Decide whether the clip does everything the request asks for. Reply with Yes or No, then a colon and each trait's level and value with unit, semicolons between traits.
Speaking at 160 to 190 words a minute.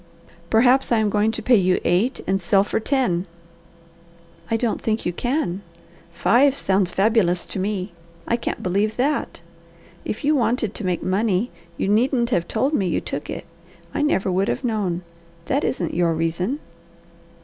Yes: average, 170 wpm